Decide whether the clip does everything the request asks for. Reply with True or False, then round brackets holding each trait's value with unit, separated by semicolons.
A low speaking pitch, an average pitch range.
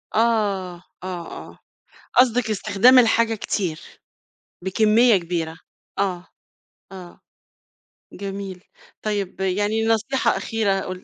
False (200 Hz; 3.2 semitones)